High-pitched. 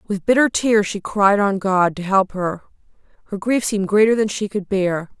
Yes: high, 200 Hz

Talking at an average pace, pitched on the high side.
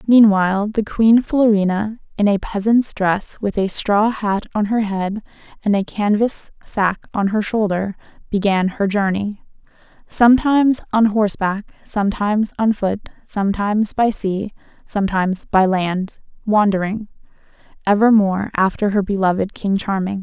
No: slow, 130 wpm; high, 205 Hz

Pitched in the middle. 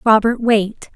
No: high, 220 Hz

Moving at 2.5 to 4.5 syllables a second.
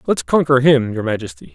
No: 5.6 syllables/s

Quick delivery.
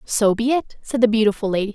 Yes: fast, 240 wpm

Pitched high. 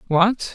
Yes: high, 195 Hz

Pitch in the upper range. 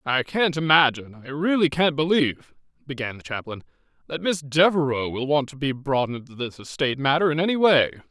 No: medium, 145 Hz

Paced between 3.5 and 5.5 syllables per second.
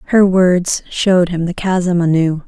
Yes: 4.2 syllables/s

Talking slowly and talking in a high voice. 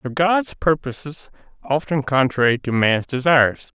No: slow, 125 wpm; medium, 140 Hz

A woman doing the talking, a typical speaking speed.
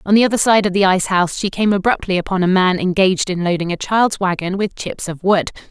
No: female; fast, 250 wpm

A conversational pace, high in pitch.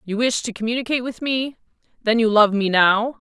Yes: average, 185 wpm; high, 230 Hz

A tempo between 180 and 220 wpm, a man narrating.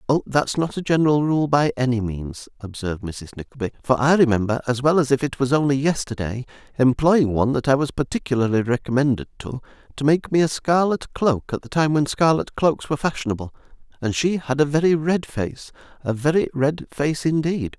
Yes: average, 190 wpm; male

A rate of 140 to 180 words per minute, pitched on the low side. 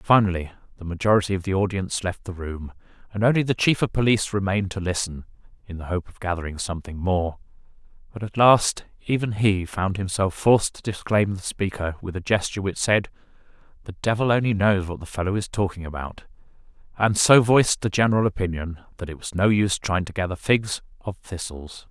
No: average, 190 wpm; very low, 95 Hz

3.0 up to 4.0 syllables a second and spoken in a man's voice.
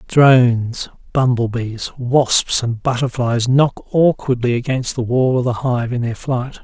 Yes: 3.9 syllables/s; male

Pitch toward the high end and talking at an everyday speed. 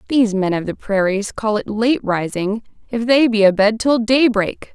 Yes: high, 215 Hz; average, 190 wpm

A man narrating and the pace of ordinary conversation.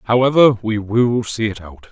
Yes: male; average, 190 wpm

